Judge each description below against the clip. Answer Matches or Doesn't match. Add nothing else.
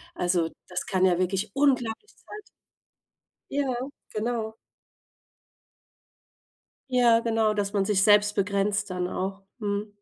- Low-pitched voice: Doesn't match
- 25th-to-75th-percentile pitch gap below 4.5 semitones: Matches